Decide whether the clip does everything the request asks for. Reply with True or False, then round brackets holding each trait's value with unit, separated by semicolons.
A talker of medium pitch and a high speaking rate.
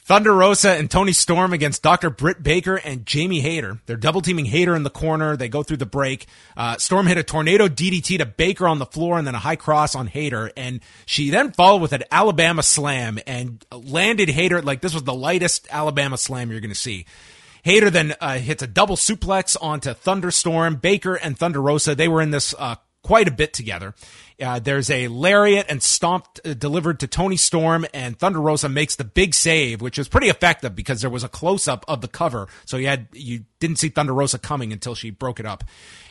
True (150 Hz; 220 wpm)